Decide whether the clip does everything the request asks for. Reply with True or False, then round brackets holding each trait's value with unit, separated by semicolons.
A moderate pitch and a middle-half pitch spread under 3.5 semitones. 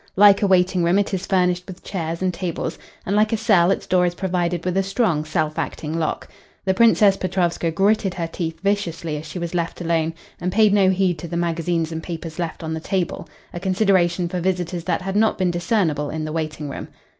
True (175 Hz; 2.4 semitones)